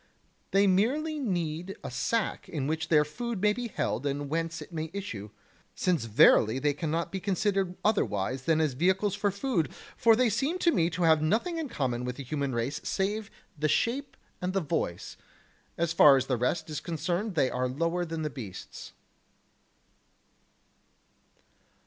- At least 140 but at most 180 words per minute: Yes, average, 170 wpm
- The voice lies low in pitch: No, medium, 165 Hz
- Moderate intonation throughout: No, wide, 5.9 semitones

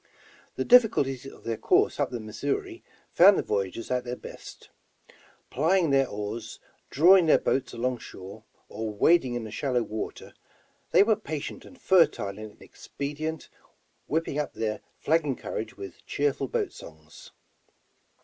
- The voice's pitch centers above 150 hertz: No, low, 130 Hz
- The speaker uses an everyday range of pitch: No, wide, 6.6 semitones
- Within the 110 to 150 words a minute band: Yes, average, 145 wpm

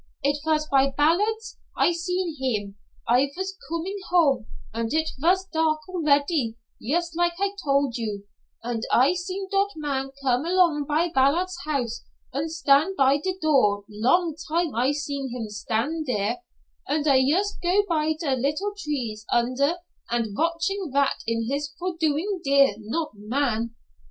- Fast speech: No, average, 155 wpm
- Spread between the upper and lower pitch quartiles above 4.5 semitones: Yes, average, 5.0 semitones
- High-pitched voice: Yes, very high, 295 Hz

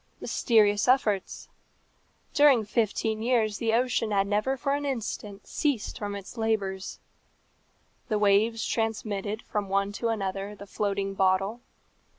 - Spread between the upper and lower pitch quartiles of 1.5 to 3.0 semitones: Yes, narrow, 2.4 semitones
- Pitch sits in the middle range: No, high, 210 Hz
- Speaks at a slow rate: Yes, slow, 130 wpm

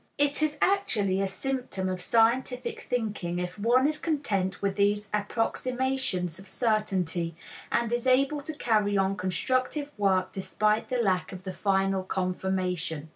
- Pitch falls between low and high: No, high, 205 Hz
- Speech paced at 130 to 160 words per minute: Yes, average, 145 wpm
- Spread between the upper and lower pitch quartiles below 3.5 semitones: No, average, 5.3 semitones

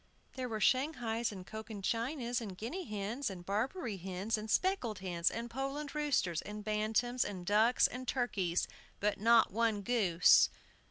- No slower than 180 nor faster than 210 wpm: No, average, 155 wpm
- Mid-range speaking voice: No, high, 220 Hz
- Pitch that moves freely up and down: No, average, 3.8 semitones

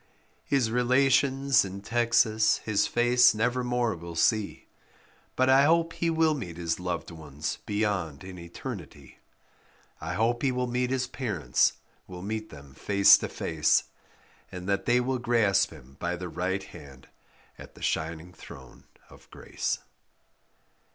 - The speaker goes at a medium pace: Yes, average, 145 wpm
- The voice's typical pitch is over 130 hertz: No, low, 110 Hz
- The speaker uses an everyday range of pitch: No, wide, 5.9 semitones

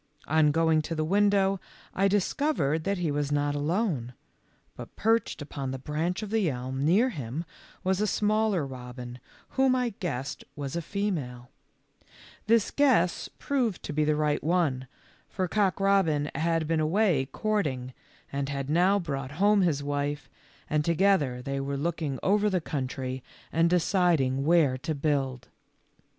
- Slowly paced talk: No, average, 165 wpm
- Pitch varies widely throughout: Yes, wide, 5.9 semitones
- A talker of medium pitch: Yes, medium, 155 Hz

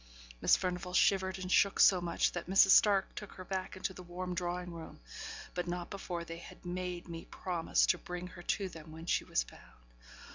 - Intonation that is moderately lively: No, narrow, 1.3 semitones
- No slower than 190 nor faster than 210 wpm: Yes, fast, 205 wpm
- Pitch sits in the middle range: Yes, medium, 180 Hz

